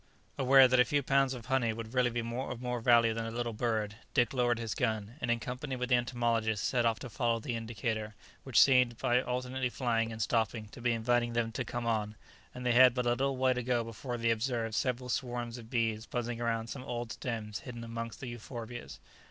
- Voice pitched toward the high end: No, low, 120 Hz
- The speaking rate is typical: No, fast, 225 wpm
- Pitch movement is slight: Yes, narrow, 1.7 semitones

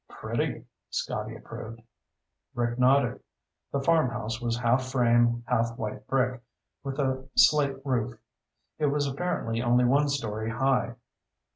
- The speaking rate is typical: No, slow, 125 wpm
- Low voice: Yes, low, 125 Hz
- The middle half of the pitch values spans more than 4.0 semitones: No, narrow, 2.5 semitones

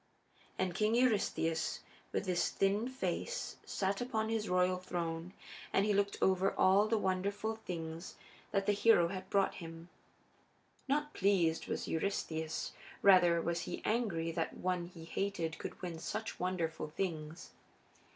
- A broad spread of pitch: No, average, 3.4 semitones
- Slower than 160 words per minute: Yes, average, 145 wpm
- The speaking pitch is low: No, medium, 185 Hz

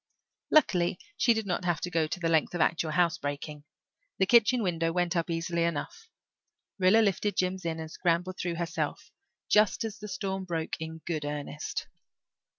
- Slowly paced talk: No, average, 170 wpm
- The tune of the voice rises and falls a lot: No, narrow, 2.6 semitones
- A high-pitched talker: No, medium, 175 Hz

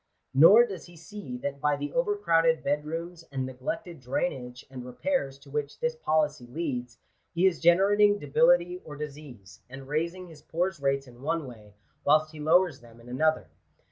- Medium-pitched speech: Yes, medium, 155 Hz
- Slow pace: No, average, 175 wpm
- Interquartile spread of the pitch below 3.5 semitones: No, average, 4.8 semitones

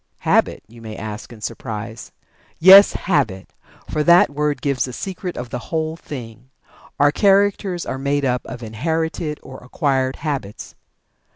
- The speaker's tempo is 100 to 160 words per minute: Yes, average, 150 wpm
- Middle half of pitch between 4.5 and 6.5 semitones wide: Yes, wide, 5.4 semitones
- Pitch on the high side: No, medium, 140 Hz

